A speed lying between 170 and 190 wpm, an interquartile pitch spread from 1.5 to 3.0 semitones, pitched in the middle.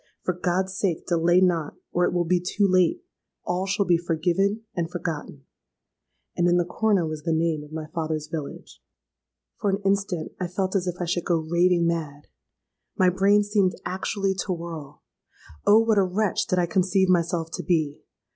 Yes: average, 180 wpm; narrow, 2.5 semitones; medium, 175 Hz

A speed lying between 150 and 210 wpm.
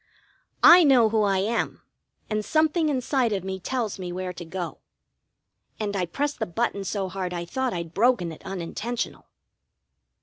Yes: average, 165 wpm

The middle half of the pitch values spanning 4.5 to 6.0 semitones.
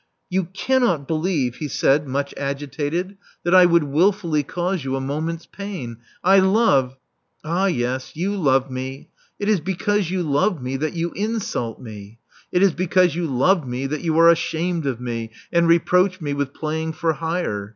Yes: average, 5.0 semitones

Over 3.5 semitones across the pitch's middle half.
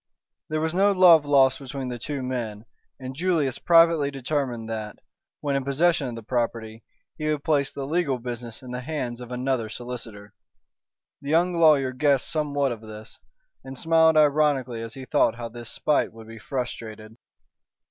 Yes: average, 4.3 semitones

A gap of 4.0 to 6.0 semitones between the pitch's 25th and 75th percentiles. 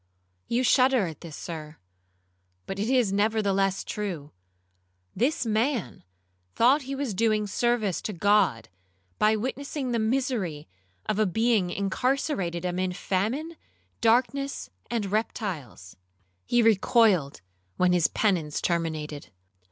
Yes: average, 5.2 semitones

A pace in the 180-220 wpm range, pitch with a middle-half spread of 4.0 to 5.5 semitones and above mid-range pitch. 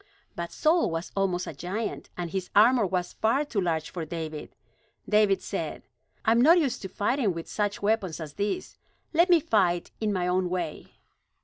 Yes: average, 185 wpm; average, 4.3 semitones; high, 195 Hz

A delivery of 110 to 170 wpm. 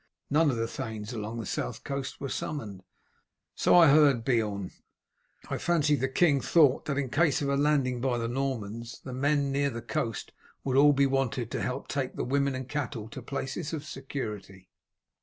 No: average, 190 wpm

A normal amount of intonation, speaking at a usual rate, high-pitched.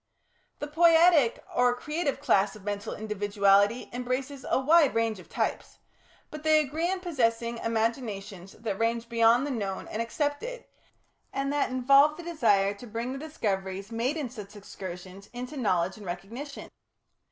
No: wide, 5.9 semitones; average, 155 wpm; high, 235 Hz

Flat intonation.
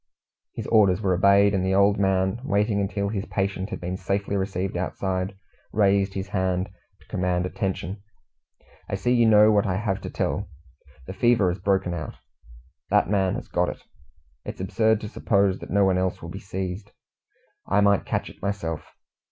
Yes: narrow, 1.5 semitones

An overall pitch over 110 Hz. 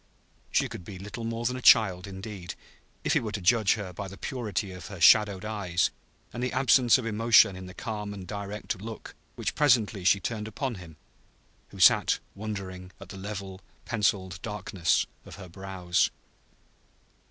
No: low, 100 Hz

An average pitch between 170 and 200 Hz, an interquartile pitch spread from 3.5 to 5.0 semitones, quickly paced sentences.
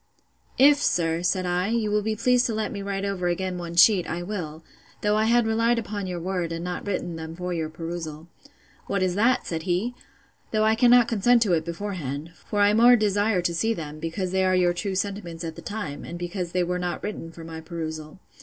Yes: medium, 185 Hz; average, 3.9 semitones; fast, 225 wpm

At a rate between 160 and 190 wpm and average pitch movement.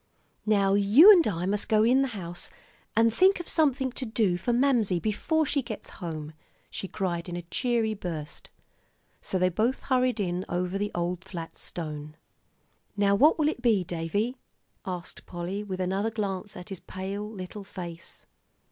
Yes: average, 170 wpm; average, 4.6 semitones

